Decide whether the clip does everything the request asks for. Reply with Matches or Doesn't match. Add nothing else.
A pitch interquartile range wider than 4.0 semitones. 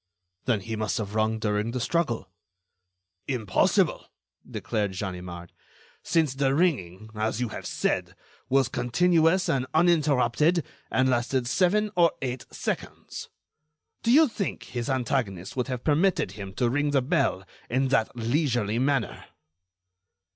Matches